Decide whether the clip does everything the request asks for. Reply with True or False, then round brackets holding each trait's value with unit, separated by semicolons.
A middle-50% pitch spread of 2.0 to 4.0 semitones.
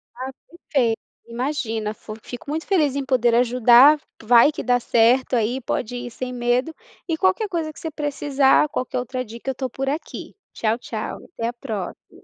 True (3.4 semitones)